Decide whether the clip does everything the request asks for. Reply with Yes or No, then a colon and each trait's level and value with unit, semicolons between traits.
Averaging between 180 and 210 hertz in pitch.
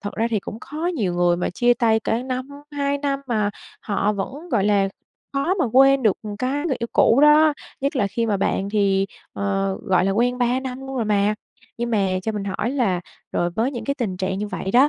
No: high, 225 Hz